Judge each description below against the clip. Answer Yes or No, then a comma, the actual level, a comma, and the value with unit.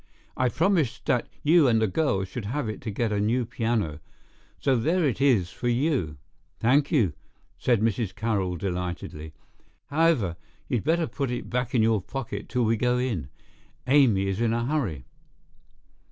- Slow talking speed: No, average, 170 wpm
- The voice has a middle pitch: No, low, 120 Hz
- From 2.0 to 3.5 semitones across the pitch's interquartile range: No, average, 5.2 semitones